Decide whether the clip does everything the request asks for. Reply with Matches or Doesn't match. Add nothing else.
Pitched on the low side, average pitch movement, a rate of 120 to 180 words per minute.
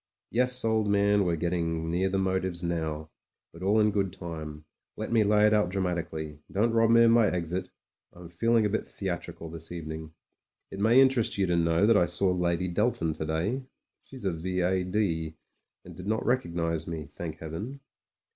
Doesn't match